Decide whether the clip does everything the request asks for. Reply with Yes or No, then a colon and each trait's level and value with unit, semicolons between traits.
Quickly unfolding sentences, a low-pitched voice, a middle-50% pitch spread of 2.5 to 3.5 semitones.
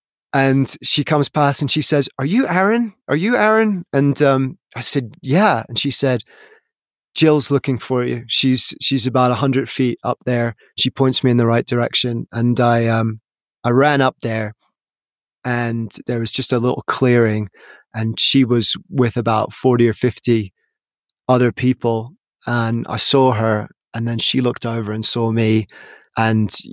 No: average, 175 wpm; low, 125 Hz; average, 3.0 semitones